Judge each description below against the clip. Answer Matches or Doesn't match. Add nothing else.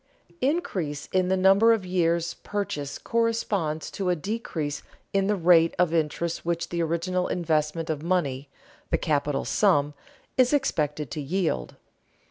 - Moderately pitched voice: Matches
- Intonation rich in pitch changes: Doesn't match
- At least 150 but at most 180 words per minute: Doesn't match